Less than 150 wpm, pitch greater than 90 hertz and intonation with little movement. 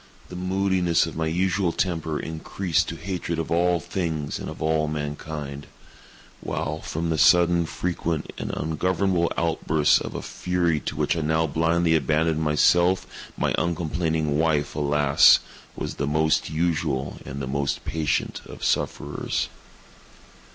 No: average, 140 wpm; very low, 80 Hz; narrow, 2.3 semitones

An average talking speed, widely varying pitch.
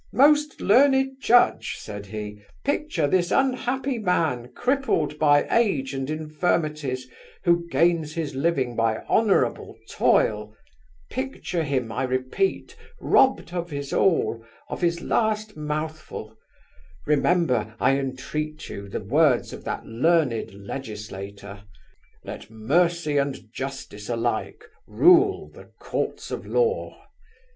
No: slow, 115 wpm; wide, 7.3 semitones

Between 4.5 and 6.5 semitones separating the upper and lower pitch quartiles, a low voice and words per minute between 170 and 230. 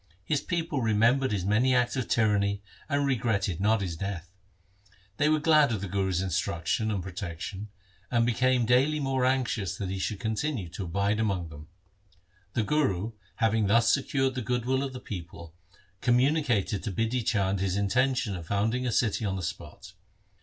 Yes: average, 4.9 semitones; low, 110 Hz; average, 175 wpm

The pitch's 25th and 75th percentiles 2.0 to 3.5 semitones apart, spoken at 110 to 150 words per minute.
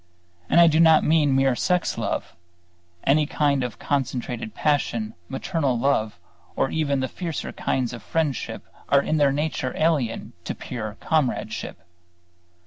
No: average, 4.0 semitones; average, 140 wpm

